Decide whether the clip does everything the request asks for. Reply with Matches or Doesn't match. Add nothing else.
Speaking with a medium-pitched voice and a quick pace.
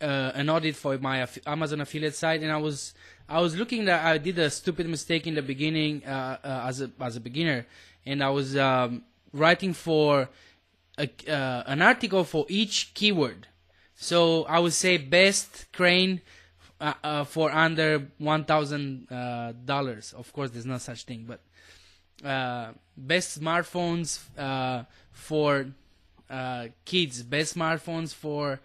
Doesn't match